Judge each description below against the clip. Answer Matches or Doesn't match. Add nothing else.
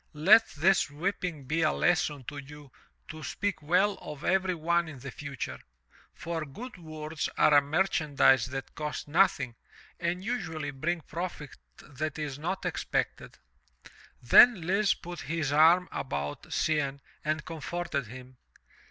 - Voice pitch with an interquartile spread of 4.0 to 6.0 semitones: Doesn't match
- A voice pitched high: Doesn't match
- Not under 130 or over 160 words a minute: Matches